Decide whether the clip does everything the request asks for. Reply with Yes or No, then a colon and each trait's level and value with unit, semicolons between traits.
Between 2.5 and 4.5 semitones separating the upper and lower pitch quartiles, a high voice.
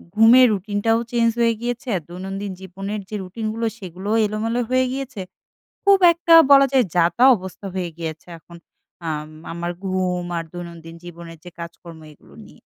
No: average, 5.0 semitones; high, 195 Hz